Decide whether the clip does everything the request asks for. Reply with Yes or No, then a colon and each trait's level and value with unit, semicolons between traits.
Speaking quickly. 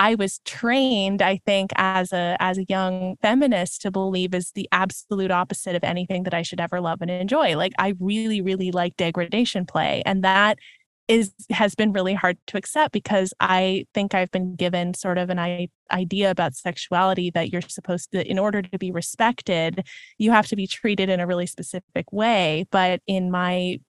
No: average, 190 wpm